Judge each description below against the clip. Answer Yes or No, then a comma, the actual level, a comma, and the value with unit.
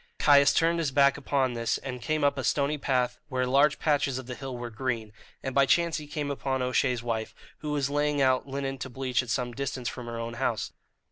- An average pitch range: No, narrow, 2.3 semitones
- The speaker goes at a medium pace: No, fast, 225 wpm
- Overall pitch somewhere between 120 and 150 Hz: Yes, low, 135 Hz